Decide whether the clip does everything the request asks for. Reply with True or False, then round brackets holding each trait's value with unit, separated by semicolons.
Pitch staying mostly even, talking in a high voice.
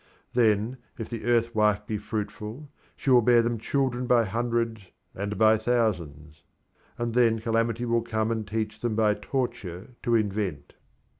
False (2.0 semitones; 110 Hz)